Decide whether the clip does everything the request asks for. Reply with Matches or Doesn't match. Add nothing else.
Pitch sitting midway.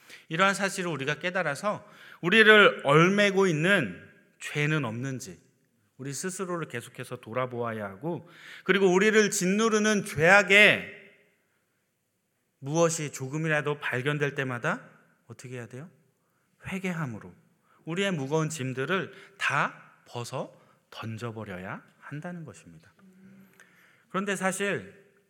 Matches